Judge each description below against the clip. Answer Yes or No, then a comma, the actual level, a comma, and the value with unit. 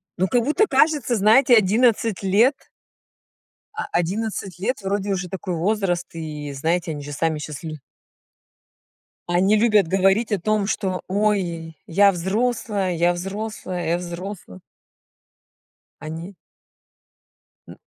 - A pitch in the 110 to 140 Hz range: No, high, 190 Hz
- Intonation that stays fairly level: No, average, 3.8 semitones